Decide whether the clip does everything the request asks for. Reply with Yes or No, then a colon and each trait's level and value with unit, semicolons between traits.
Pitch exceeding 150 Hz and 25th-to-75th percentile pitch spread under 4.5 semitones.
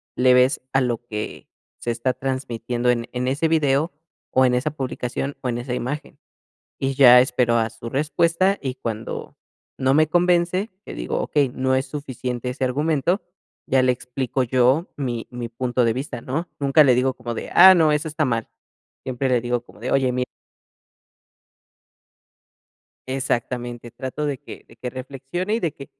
No: low, 130 Hz; average, 2.8 semitones